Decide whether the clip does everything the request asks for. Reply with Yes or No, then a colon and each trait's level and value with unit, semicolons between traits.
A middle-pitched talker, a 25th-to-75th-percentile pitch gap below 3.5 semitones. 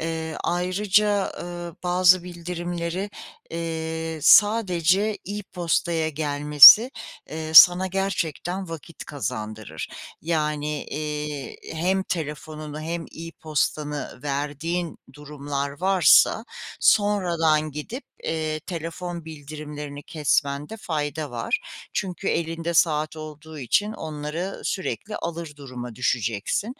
Yes: medium, 160 Hz; average, 3.0 semitones